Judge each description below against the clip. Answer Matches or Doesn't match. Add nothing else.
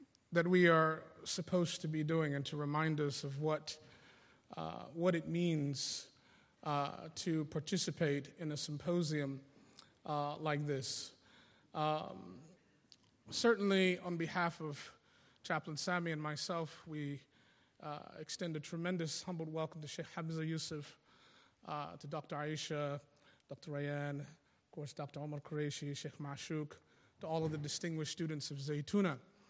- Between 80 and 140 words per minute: Matches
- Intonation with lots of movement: Doesn't match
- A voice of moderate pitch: Matches